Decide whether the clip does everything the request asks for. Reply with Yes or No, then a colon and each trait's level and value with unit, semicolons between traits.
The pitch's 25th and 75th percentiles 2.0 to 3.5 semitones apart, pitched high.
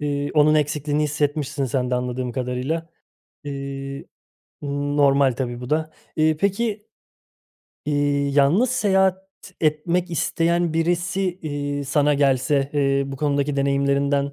No: narrow, 2.4 semitones; medium, 145 Hz